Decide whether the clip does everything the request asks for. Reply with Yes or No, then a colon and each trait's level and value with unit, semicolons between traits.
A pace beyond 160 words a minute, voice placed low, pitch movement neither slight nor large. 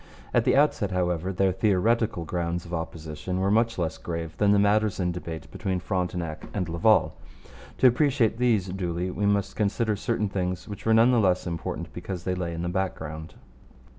Yes: average, 185 wpm; very low, 95 Hz; average, 3.3 semitones